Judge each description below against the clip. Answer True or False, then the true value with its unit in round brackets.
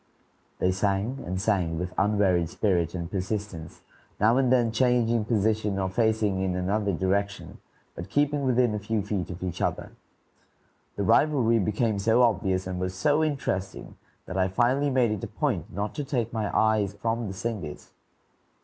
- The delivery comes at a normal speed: True (165 wpm)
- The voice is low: True (105 Hz)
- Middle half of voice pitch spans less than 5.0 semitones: True (3.8 semitones)